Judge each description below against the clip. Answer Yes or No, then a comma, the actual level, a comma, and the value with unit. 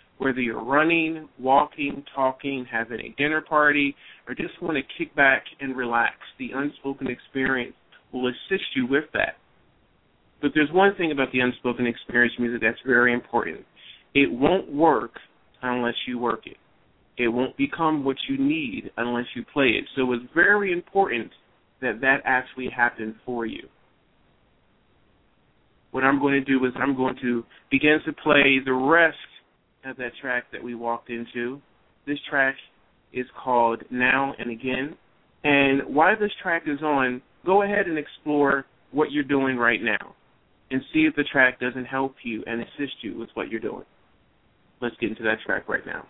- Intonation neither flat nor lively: Yes, average, 3.3 semitones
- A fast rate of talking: No, average, 170 wpm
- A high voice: No, low, 135 Hz